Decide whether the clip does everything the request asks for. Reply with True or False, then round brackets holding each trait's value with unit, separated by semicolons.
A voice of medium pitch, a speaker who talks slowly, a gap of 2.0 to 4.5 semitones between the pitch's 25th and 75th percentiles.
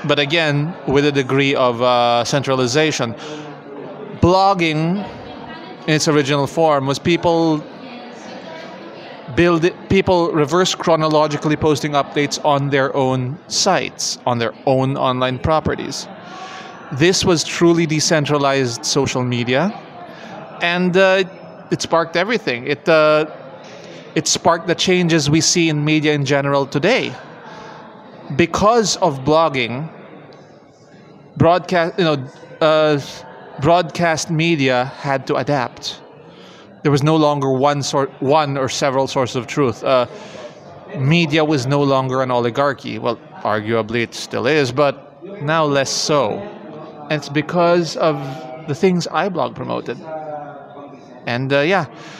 True (150 Hz; 125 wpm; 3.6 semitones)